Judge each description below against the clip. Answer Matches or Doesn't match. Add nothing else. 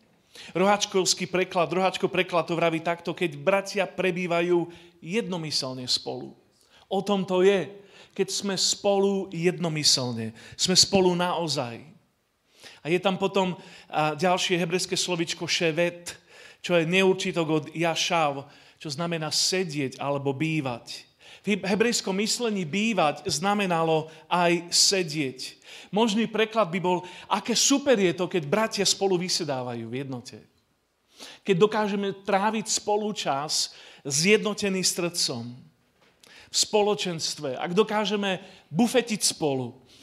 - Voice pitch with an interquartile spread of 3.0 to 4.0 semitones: Matches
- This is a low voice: Doesn't match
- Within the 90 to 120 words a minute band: Matches